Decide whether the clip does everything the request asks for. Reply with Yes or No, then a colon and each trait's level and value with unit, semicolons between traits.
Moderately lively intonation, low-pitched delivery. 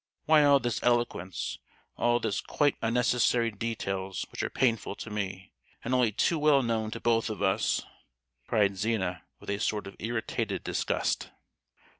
Yes: average, 3.3 semitones; low, 115 Hz